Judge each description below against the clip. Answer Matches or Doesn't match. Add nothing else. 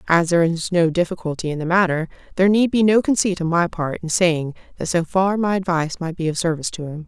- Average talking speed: Doesn't match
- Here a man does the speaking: Doesn't match